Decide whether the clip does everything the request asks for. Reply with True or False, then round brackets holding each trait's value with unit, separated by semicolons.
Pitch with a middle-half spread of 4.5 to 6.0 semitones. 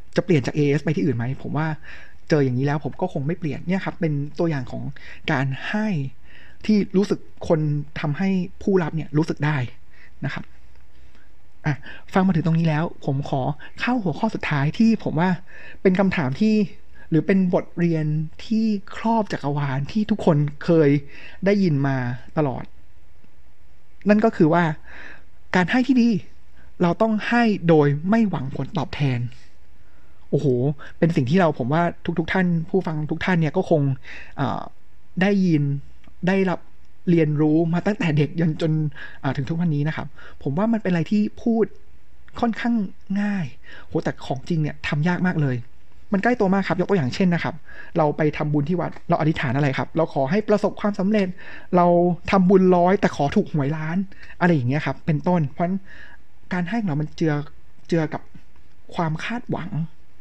True (4.9 semitones)